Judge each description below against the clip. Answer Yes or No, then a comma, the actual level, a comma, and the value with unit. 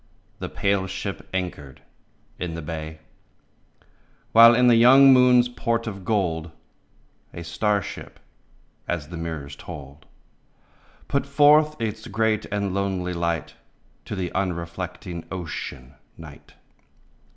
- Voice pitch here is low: Yes, very low, 95 Hz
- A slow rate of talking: Yes, slow, 125 wpm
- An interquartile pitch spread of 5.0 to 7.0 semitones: Yes, wide, 5.4 semitones